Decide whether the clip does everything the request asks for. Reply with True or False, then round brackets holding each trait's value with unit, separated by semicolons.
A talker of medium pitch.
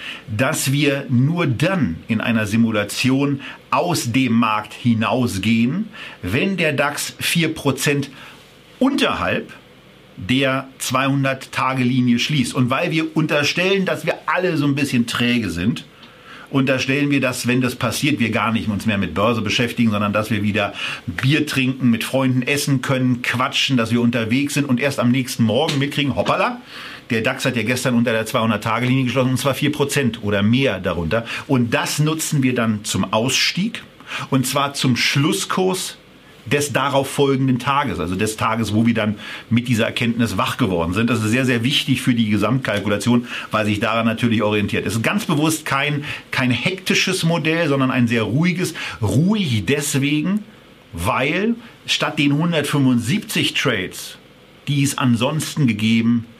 False (130 Hz)